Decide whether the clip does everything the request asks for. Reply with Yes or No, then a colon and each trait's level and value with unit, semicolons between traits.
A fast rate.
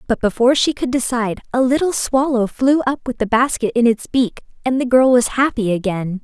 Yes: fast, 210 wpm